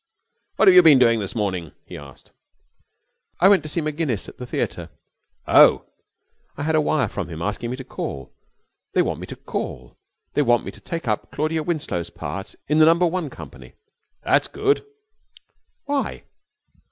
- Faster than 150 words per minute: Yes, average, 160 wpm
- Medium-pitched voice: Yes, medium, 145 Hz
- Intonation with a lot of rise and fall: Yes, wide, 8.0 semitones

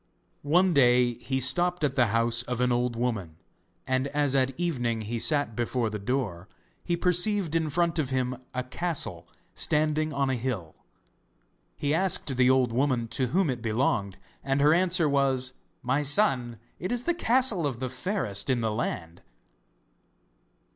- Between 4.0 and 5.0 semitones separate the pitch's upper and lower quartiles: Yes, average, 4.5 semitones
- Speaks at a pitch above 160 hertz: No, low, 130 Hz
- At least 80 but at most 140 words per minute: No, average, 165 wpm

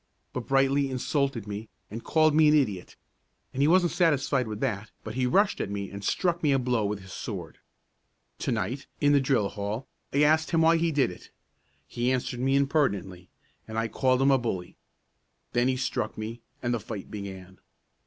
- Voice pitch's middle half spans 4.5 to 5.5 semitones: Yes, average, 5.1 semitones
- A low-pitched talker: Yes, low, 125 Hz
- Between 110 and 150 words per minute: No, average, 195 wpm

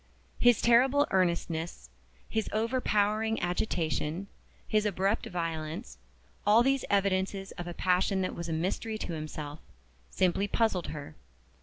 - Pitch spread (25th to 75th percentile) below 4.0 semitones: No, average, 4.3 semitones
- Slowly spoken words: Yes, slow, 125 wpm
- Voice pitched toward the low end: No, high, 190 Hz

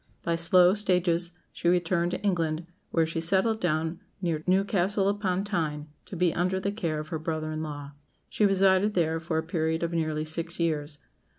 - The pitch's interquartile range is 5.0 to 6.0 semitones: No, average, 2.8 semitones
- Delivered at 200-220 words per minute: No, average, 185 wpm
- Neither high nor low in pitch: Yes, medium, 170 Hz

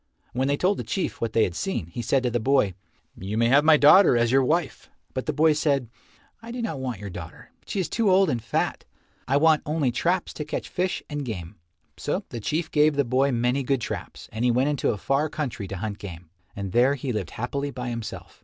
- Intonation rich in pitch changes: No, average, 4.7 semitones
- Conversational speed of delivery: No, fast, 240 wpm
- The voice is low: Yes, low, 130 Hz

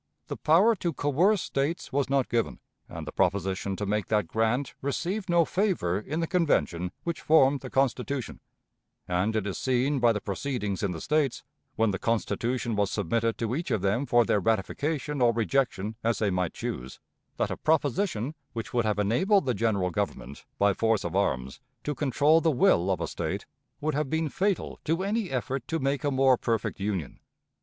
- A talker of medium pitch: No, low, 120 Hz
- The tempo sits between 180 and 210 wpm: Yes, average, 190 wpm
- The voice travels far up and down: Yes, wide, 6.4 semitones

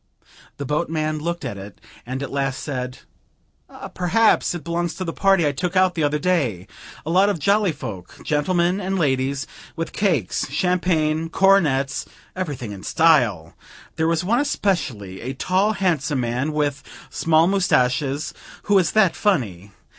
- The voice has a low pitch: No, medium, 155 Hz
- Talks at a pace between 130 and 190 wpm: Yes, average, 155 wpm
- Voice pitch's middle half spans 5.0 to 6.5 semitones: Yes, average, 5.3 semitones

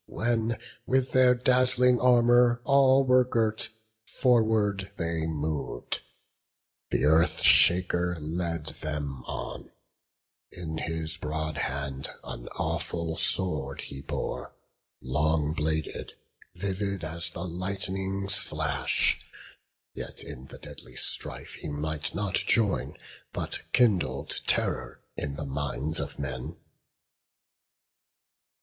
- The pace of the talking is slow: Yes, slow, 105 wpm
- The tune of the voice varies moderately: No, wide, 6.5 semitones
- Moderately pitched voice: No, very low, 85 Hz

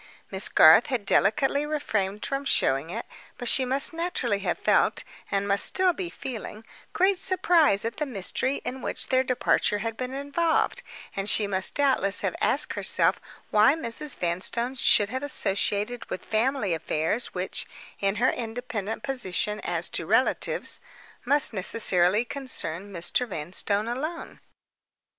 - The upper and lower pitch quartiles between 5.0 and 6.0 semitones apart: Yes, wide, 5.4 semitones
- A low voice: No, high, 230 Hz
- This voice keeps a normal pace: Yes, average, 150 wpm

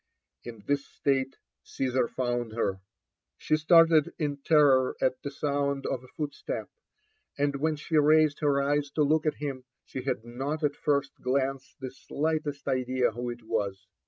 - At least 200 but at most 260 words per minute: No, average, 165 wpm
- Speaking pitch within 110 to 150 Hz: Yes, medium, 140 Hz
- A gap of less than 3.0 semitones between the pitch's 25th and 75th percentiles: Yes, narrow, 2.5 semitones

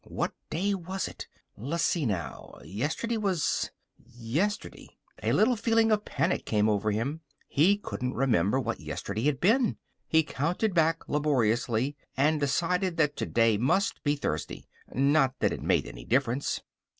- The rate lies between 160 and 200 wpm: No, average, 145 wpm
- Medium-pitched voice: Yes, medium, 145 Hz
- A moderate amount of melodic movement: No, wide, 7.4 semitones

